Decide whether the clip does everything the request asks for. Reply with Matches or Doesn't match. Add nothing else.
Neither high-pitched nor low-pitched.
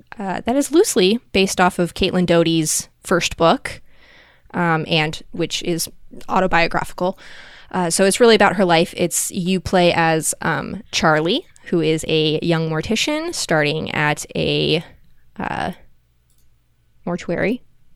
Matches